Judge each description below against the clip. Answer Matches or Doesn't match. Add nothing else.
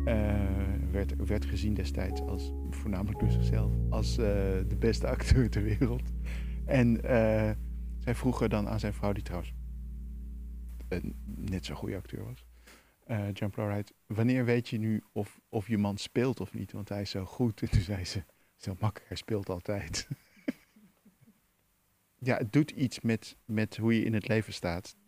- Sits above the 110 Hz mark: Doesn't match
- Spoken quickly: Doesn't match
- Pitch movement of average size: Doesn't match